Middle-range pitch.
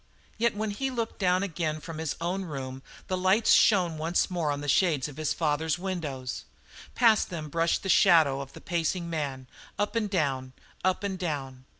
Yes: medium, 165 Hz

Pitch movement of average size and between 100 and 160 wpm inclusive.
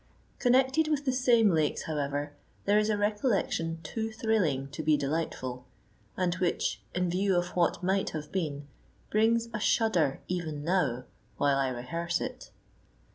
No: wide, 6.6 semitones; average, 150 wpm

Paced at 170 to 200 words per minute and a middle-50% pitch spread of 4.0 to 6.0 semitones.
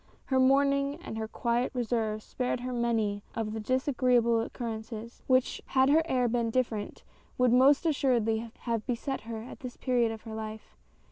No: average, 180 wpm; narrow, 2.5 semitones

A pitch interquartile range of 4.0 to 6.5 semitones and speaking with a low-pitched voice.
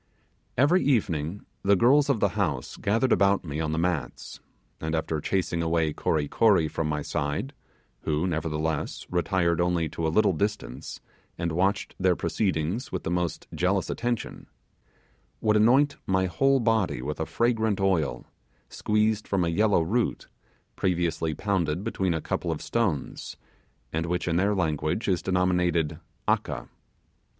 Yes: average, 4.8 semitones; very low, 90 Hz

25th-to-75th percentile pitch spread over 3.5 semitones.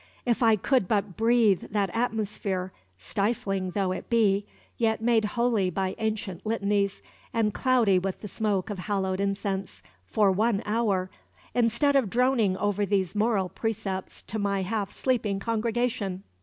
No: average, 2.8 semitones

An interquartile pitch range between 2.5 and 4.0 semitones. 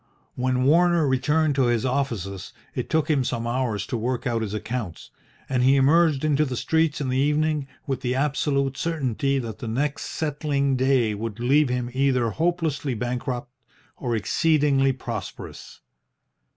Yes: average, 3.4 semitones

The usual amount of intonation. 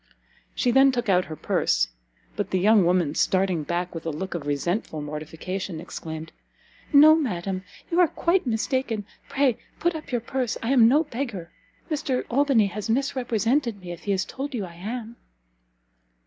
No: wide, 6.9 semitones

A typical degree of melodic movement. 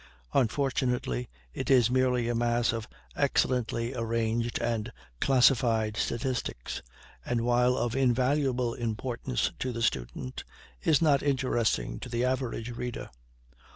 No: narrow, 1.9 semitones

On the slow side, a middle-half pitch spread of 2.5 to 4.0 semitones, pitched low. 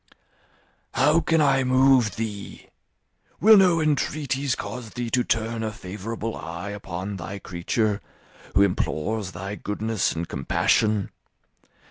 No: slow, 120 wpm; average, 4.8 semitones; low, 110 Hz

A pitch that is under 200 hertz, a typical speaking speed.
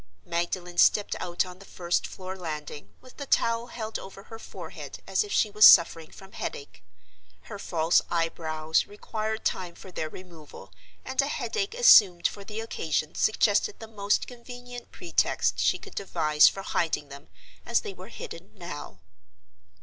Yes: high, 190 Hz; average, 160 wpm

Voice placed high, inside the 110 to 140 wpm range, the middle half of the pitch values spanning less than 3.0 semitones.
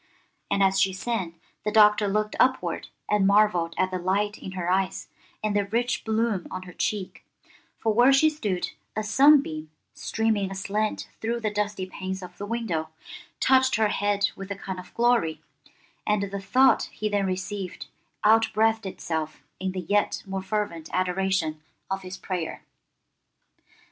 No: high, 200 Hz; average, 160 wpm; narrow, 2.6 semitones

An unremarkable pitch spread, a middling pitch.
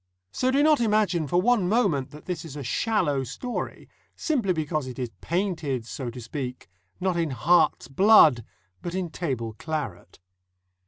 No: wide, 6.8 semitones; medium, 160 Hz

